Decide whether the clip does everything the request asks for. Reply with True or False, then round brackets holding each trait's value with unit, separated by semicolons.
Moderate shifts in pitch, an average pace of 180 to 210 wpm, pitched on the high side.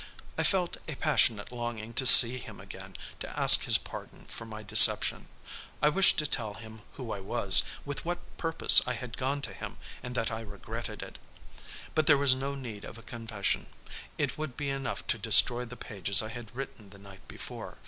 False (4.0 semitones; 200 wpm; 120 Hz)